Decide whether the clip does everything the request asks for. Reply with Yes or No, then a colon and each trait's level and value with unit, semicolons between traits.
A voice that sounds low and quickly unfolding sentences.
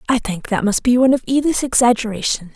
No: high, 240 Hz; fast, 210 wpm